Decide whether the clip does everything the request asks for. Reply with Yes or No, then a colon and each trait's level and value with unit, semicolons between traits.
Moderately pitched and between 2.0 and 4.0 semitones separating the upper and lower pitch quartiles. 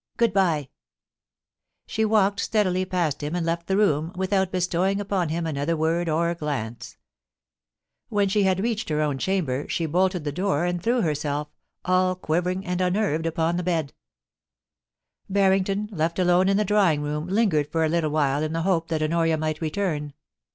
Yes: medium, 170 Hz; average, 3.5 semitones